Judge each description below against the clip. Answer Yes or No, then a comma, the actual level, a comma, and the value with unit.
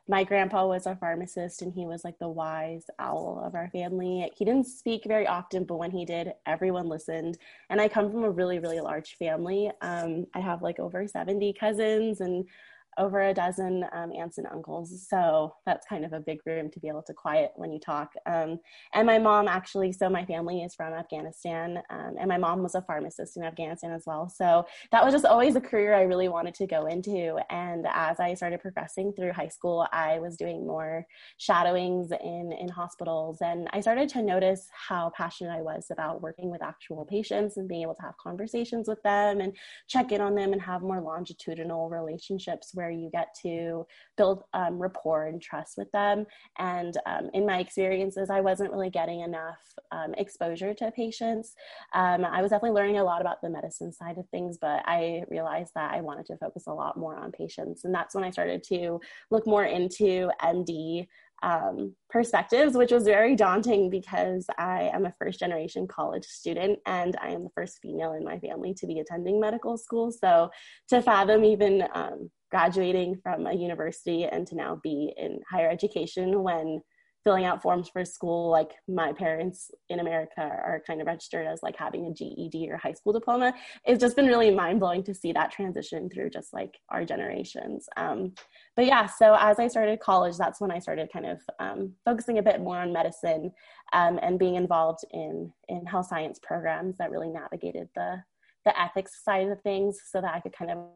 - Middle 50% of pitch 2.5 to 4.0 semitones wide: Yes, average, 3.4 semitones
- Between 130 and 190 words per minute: No, average, 200 wpm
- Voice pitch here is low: No, medium, 180 Hz